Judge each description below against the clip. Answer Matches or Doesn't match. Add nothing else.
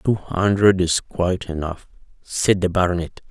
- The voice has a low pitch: Matches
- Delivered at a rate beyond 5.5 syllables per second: Doesn't match